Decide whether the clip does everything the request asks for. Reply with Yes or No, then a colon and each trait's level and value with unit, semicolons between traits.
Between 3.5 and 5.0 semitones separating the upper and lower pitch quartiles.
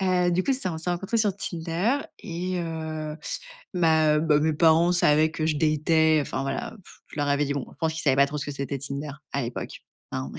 No: average, 2.9 semitones